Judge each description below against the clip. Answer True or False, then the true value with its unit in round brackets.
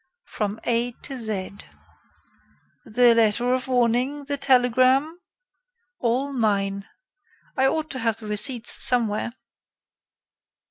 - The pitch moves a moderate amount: True (3.1 semitones)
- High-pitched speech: True (245 Hz)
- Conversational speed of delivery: False (105 wpm)